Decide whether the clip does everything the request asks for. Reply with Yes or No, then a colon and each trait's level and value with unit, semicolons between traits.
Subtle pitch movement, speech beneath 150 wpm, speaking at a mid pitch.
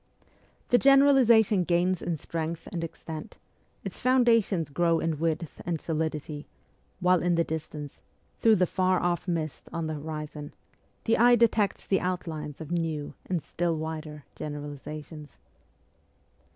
No: average, 3.2 semitones; slow, 135 wpm; medium, 165 Hz